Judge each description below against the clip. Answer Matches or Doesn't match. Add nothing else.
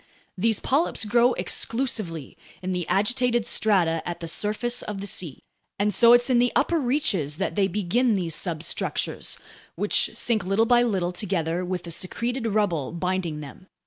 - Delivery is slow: Doesn't match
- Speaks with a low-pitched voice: Doesn't match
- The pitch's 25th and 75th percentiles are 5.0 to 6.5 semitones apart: Matches